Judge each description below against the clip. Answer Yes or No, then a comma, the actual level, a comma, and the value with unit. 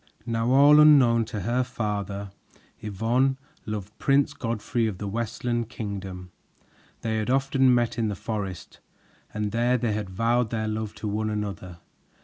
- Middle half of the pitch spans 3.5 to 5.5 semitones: No, average, 2.8 semitones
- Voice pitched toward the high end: No, low, 110 Hz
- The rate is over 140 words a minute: Yes, average, 150 wpm